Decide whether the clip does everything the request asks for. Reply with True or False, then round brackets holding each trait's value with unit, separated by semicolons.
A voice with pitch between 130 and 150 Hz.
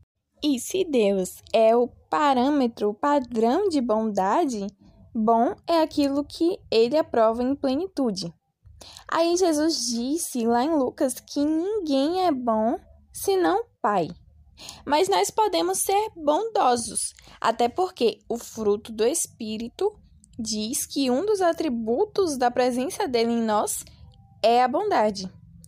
False (260 Hz)